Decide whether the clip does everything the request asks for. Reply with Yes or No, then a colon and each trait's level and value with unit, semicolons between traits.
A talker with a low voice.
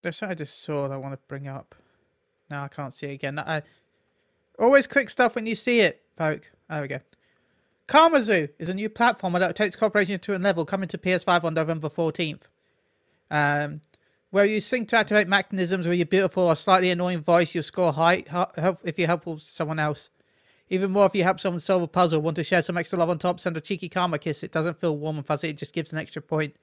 No: medium, 175 Hz